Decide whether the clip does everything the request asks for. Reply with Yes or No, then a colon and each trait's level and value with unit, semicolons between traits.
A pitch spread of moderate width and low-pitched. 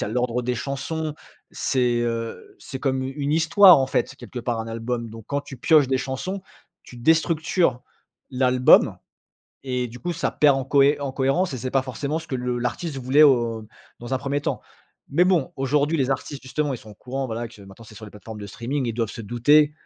Yes: average, 3.3 semitones; low, 130 Hz